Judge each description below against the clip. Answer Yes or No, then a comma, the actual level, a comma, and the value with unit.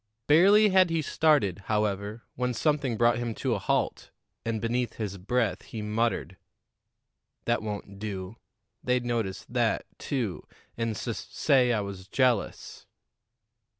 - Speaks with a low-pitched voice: Yes, low, 115 Hz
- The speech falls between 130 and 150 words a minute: Yes, slow, 135 wpm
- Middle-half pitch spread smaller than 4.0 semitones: Yes, average, 3.6 semitones